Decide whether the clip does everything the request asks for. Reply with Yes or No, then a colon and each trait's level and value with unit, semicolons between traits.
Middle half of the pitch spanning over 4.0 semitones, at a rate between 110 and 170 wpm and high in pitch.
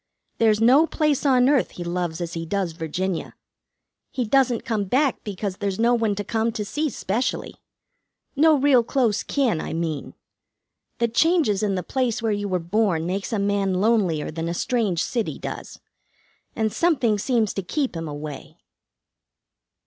Yes: wide, 5.4 semitones; average, 165 wpm; high, 210 Hz